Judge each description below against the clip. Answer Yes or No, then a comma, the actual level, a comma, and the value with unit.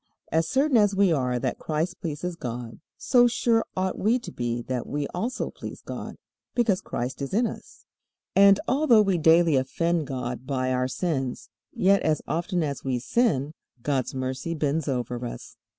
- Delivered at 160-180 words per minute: Yes, average, 170 wpm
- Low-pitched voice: No, medium, 160 Hz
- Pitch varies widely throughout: Yes, wide, 7.1 semitones